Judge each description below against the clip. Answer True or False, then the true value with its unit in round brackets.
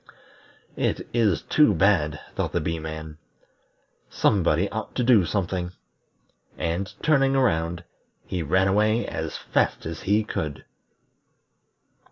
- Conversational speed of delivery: False (120 wpm)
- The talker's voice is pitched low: True (95 Hz)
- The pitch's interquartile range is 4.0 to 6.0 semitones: True (4.7 semitones)